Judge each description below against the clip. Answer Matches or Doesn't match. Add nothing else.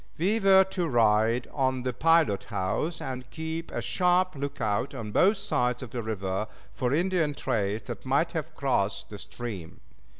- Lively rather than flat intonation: Matches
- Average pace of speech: Matches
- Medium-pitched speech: Doesn't match